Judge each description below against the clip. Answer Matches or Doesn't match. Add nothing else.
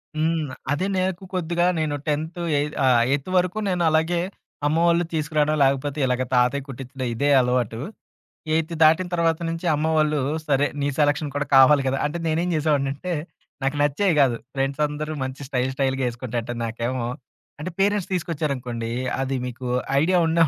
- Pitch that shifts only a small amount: Doesn't match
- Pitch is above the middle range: Doesn't match